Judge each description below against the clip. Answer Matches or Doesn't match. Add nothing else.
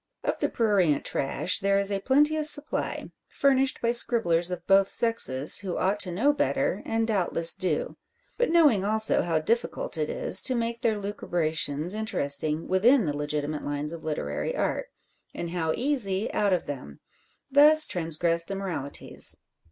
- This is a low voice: Doesn't match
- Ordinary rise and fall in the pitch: Doesn't match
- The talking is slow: Doesn't match